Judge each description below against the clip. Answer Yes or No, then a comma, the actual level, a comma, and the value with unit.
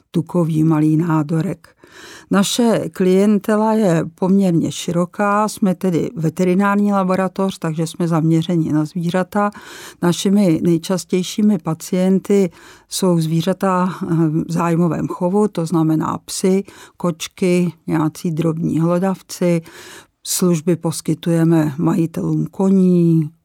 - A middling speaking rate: No, slow, 90 wpm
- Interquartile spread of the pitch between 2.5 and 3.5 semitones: Yes, average, 2.8 semitones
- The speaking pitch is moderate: Yes, medium, 175 Hz